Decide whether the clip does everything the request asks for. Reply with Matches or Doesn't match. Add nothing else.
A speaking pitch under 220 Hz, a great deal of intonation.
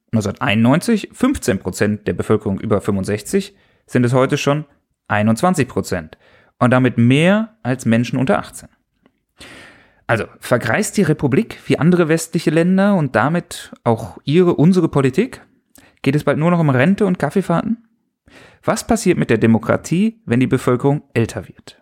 Matches